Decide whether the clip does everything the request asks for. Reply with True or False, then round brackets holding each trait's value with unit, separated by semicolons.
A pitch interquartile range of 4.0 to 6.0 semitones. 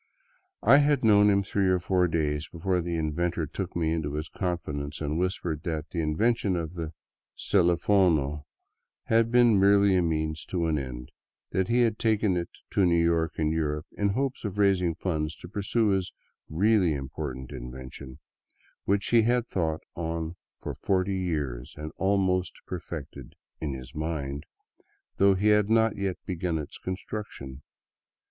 True (4.3 semitones)